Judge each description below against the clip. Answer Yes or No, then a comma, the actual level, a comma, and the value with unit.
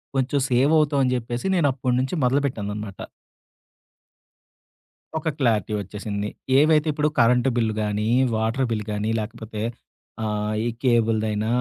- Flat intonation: No, average, 3.8 semitones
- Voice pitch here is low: Yes, low, 115 Hz